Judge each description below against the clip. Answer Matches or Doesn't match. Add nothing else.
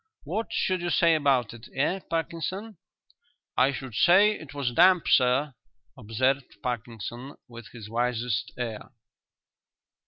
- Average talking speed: Doesn't match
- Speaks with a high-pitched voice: Doesn't match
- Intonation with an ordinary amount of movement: Doesn't match